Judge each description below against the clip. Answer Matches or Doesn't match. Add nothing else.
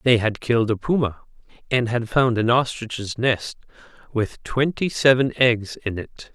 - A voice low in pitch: Matches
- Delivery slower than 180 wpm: Matches